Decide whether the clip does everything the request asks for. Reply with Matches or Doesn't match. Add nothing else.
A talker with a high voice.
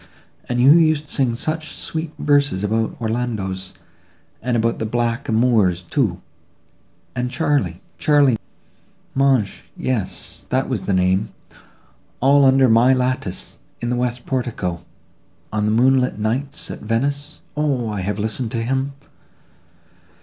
Doesn't match